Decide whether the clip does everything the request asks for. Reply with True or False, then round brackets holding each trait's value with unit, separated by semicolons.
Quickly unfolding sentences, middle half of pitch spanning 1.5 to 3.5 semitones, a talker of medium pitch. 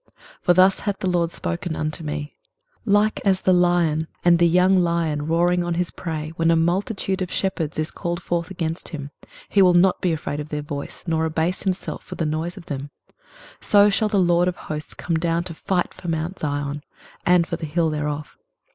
True (210 wpm; 2.4 semitones; 170 Hz)